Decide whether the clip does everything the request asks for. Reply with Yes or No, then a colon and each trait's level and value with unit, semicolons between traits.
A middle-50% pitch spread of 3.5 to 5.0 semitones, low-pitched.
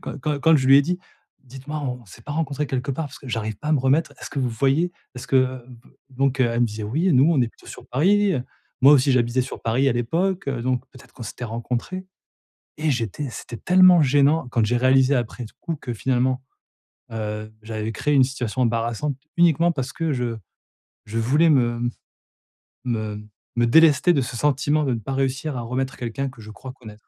Yes: average, 3.8 semitones; low, 130 Hz